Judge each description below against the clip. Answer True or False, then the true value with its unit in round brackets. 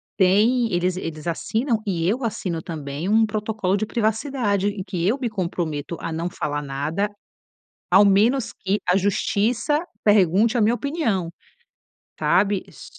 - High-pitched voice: True (200 Hz)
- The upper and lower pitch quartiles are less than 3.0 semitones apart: False (4.2 semitones)